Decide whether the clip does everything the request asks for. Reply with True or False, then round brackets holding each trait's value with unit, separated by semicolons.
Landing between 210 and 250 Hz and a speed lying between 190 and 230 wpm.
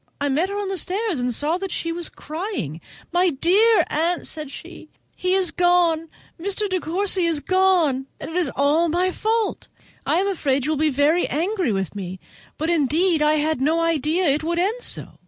False (335 Hz; 195 wpm)